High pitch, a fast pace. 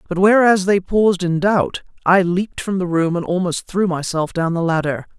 No: medium, 180 Hz; fast, 210 wpm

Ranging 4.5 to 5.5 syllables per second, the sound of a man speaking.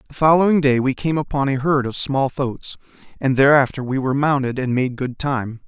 Yes: 5.4 syllables/s; male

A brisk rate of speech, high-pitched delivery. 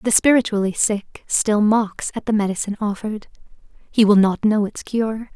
No: average, 170 wpm; high, 210 Hz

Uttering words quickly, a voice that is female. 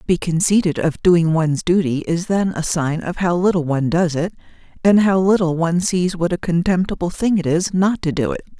Yes: fast, 225 wpm; female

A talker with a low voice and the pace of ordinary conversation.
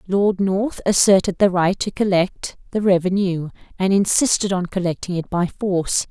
No: high, 190 Hz; average, 155 wpm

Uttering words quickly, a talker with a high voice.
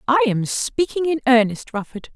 No: average, 165 wpm; very high, 255 Hz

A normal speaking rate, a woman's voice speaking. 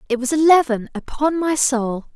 Yes: average, 165 wpm; female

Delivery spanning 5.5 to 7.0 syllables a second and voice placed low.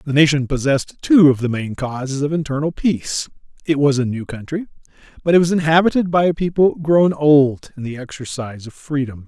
No: 5.6 syllables/s; medium, 145 Hz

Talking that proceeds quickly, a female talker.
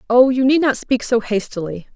Yes: fast, 215 wpm; female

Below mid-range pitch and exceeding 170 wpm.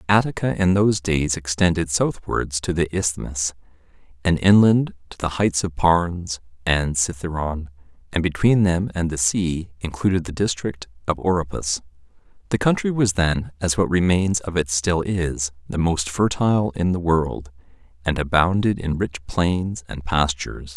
No: very low, 85 Hz; average, 155 wpm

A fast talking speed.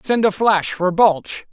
No: average, 195 wpm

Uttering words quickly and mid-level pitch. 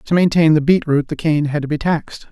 Yes: fast, 285 wpm; medium, 155 Hz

